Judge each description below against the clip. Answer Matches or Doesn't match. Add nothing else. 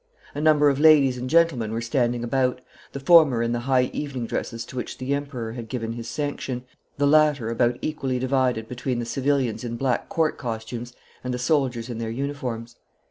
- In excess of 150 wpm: Matches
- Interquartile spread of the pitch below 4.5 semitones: Matches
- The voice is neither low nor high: Doesn't match